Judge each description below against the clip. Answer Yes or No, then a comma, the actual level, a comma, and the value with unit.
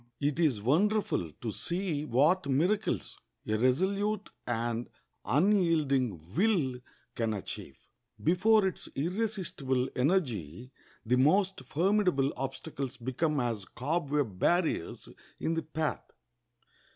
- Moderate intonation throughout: No, wide, 6.5 semitones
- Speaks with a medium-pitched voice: Yes, medium, 145 Hz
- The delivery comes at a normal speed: No, slow, 105 wpm